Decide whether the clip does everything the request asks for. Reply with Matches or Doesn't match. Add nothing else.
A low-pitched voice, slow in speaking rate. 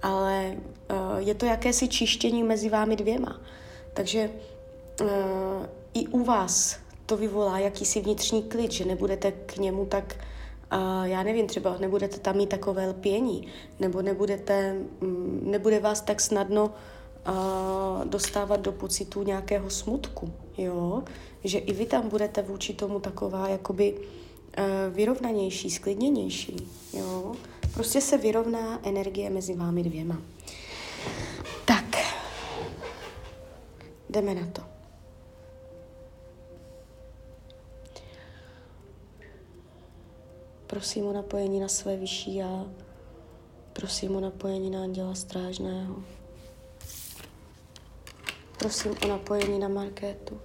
Doesn't match